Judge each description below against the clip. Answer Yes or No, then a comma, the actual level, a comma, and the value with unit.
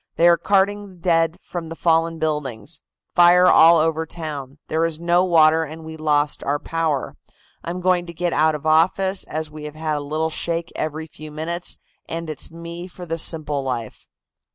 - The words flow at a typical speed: Yes, average, 185 wpm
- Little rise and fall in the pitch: Yes, narrow, 1.9 semitones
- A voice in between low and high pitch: Yes, medium, 160 Hz